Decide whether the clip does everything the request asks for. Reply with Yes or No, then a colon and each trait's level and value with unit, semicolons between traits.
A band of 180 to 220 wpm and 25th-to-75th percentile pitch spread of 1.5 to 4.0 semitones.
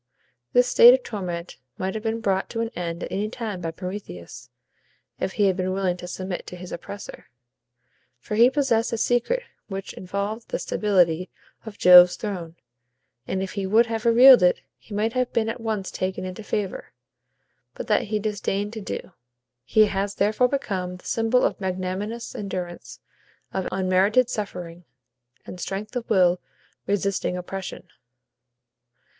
No: average, 160 wpm; average, 3.4 semitones